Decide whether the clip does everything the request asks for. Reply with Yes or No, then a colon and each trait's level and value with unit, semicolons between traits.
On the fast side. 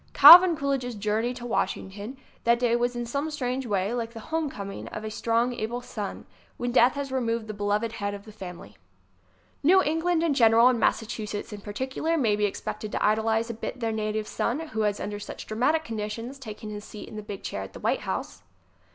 Yes: fast, 210 wpm